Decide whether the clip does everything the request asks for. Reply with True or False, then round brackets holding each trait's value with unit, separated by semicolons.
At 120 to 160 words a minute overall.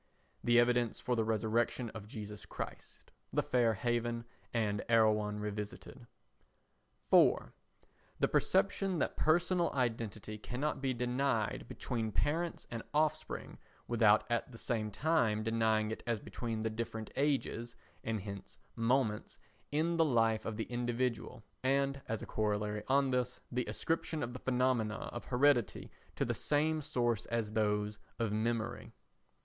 True (140 wpm)